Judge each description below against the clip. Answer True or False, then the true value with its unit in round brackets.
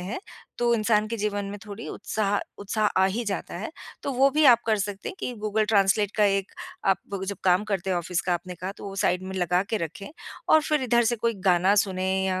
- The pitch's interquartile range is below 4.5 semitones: True (2.6 semitones)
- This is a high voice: True (200 Hz)